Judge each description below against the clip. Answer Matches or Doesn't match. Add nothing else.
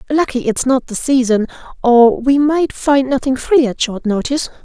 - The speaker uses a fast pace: Doesn't match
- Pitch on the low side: Doesn't match